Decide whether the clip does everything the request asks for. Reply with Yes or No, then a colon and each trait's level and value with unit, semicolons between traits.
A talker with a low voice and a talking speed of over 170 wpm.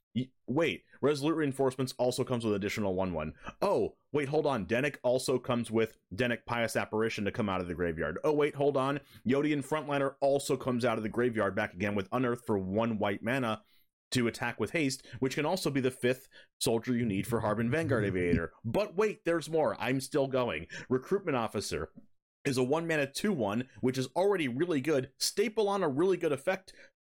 Yes: low, 125 Hz; average, 195 wpm